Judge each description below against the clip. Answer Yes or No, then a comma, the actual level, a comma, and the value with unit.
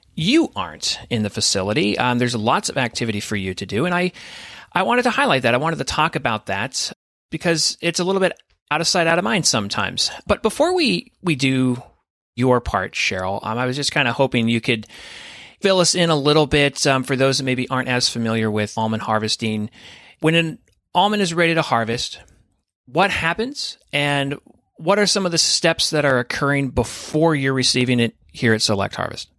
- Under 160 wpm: No, fast, 205 wpm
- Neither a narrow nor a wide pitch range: No, wide, 6.6 semitones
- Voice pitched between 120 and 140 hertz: Yes, low, 135 Hz